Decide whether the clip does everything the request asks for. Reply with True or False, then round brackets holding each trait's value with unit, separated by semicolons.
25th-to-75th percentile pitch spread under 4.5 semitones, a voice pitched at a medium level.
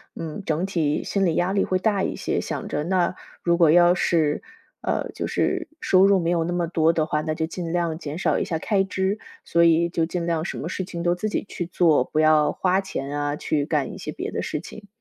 True (2.8 semitones; 170 Hz)